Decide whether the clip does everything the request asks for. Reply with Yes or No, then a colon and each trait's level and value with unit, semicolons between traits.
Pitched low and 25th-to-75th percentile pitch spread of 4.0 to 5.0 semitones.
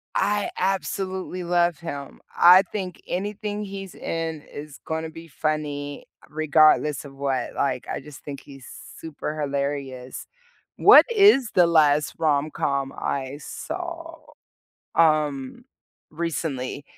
No: medium, 155 Hz; average, 4.4 semitones